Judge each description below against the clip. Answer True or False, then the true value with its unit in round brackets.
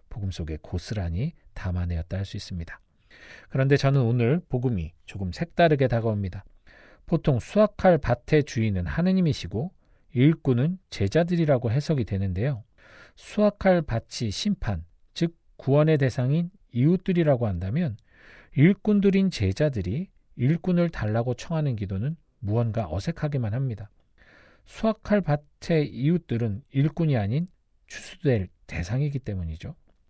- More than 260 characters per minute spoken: True (300 characters per minute)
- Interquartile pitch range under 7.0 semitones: False (8.0 semitones)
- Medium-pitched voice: False (130 Hz)